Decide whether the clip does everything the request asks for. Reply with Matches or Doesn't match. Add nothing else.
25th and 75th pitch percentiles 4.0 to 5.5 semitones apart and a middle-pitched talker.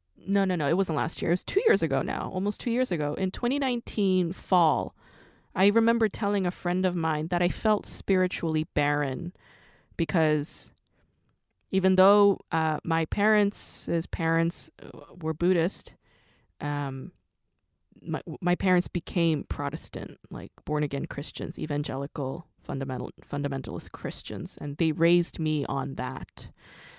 Matches